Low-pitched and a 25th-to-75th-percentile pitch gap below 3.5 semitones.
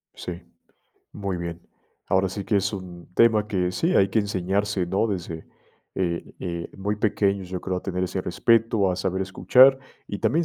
Yes: very low, 95 Hz; narrow, 2.4 semitones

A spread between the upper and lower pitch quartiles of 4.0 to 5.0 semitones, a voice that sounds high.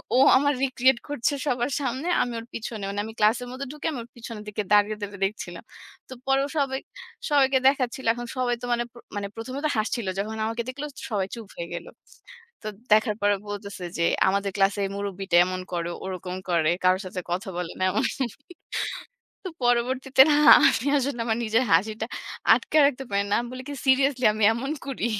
Yes: average, 4.5 semitones; high, 230 Hz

